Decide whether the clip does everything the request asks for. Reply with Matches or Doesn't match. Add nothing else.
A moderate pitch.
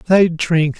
Matches